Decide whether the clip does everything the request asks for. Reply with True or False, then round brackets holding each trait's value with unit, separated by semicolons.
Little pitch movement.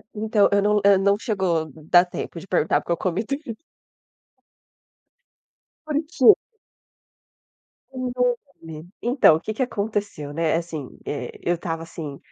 False (5.2 semitones)